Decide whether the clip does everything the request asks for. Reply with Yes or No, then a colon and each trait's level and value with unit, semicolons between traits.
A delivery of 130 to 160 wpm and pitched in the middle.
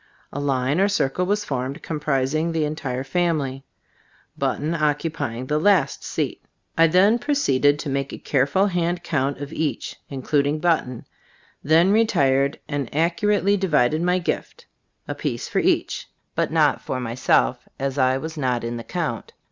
Yes: average, 155 wpm; medium, 150 Hz